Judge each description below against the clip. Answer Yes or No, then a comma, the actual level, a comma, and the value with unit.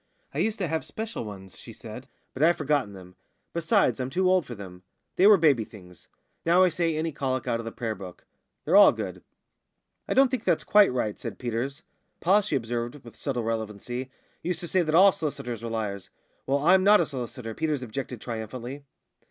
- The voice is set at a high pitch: No, low, 130 Hz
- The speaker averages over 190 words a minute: Yes, average, 200 wpm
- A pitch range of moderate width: No, wide, 7.0 semitones